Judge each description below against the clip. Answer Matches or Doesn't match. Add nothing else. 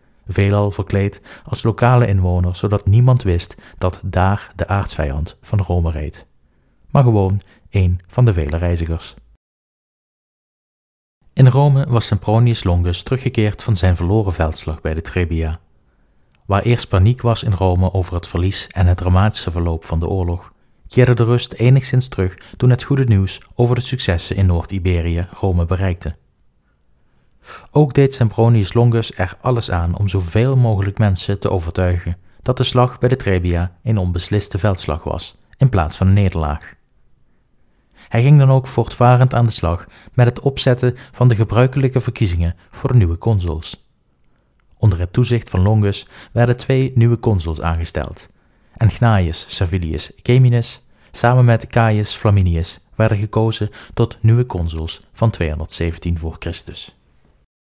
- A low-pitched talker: Matches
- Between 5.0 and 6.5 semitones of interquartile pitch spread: Matches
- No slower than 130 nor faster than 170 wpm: Matches